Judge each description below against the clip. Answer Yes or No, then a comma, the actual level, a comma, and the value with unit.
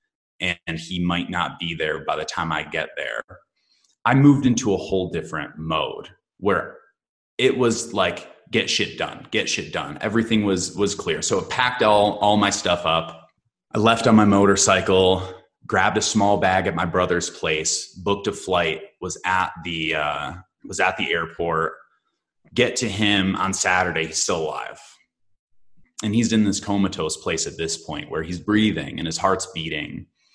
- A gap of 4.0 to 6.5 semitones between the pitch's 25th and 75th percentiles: No, average, 3.3 semitones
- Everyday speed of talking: Yes, average, 175 wpm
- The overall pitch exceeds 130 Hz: No, very low, 95 Hz